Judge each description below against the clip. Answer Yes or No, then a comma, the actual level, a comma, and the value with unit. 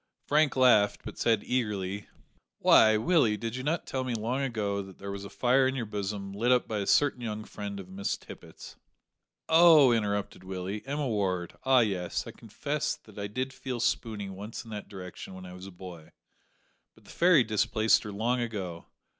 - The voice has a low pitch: Yes, low, 105 Hz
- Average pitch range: Yes, average, 4.2 semitones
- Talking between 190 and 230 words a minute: Yes, average, 195 wpm